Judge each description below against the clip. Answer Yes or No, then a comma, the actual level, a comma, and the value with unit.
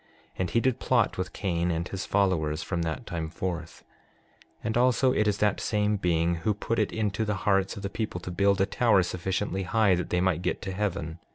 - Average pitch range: Yes, average, 3.1 semitones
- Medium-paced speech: No, fast, 220 wpm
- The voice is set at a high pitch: No, very low, 95 Hz